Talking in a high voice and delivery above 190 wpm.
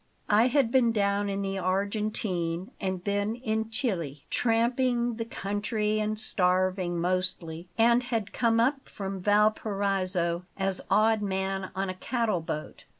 No: high, 205 Hz; average, 140 wpm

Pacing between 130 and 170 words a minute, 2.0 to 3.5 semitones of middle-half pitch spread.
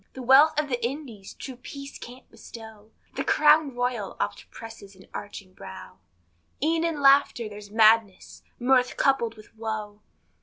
No: average, 150 wpm; average, 4.5 semitones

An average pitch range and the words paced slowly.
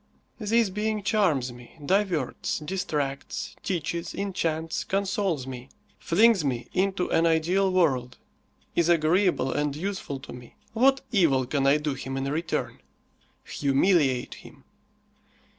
No: wide, 6.0 semitones; slow, 125 wpm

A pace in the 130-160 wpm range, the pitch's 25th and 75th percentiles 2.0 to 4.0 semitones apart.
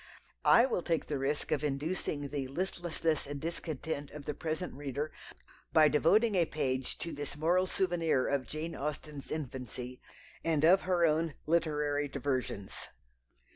Yes: average, 145 wpm; average, 2.8 semitones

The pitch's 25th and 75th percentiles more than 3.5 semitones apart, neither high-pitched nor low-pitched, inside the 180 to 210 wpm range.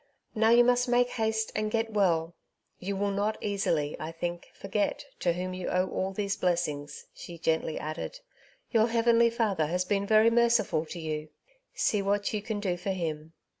No: average, 4.5 semitones; high, 200 Hz; average, 185 wpm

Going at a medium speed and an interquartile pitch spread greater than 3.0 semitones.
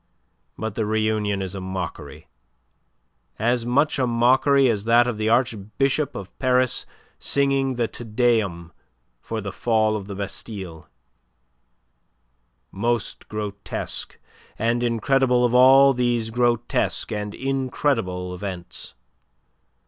No: slow, 115 wpm; average, 3.6 semitones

